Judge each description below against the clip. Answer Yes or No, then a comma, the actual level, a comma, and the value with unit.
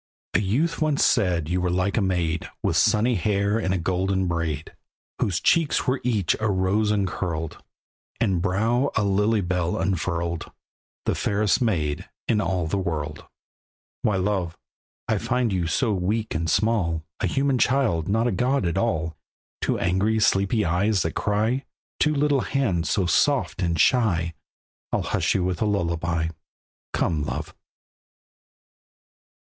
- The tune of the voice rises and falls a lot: No, average, 4.4 semitones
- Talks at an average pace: Yes, average, 150 wpm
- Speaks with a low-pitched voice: Yes, very low, 95 Hz